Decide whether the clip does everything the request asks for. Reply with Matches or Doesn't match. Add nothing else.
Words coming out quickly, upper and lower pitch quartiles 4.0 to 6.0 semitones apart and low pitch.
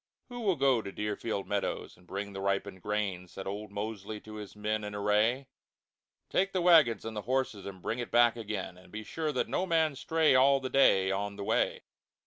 Matches